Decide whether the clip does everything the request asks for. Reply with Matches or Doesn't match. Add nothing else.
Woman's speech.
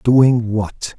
Doesn't match